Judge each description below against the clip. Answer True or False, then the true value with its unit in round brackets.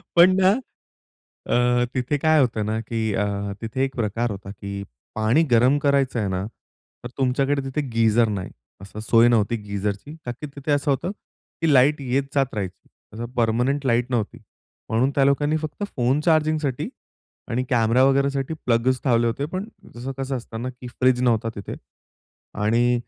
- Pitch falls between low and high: False (125 Hz)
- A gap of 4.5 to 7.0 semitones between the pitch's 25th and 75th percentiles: False (3.6 semitones)